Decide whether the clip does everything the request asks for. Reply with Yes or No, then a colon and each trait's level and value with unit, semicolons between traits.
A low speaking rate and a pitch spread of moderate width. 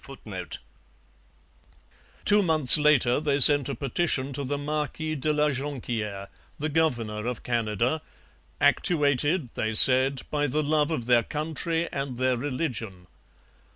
Yes: slow, 130 wpm; average, 3.7 semitones